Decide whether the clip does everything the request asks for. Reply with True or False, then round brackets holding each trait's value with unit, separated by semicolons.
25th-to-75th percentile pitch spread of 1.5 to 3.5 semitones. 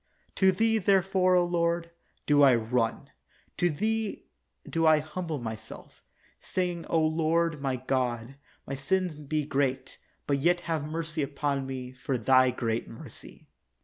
False (4.6 semitones)